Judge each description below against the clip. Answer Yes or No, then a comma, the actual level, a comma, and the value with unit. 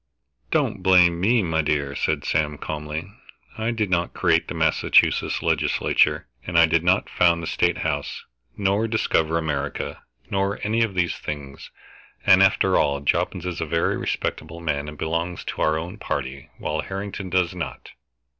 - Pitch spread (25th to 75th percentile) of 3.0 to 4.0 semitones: Yes, average, 3.7 semitones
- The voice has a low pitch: Yes, very low, 85 Hz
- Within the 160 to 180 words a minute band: Yes, average, 165 wpm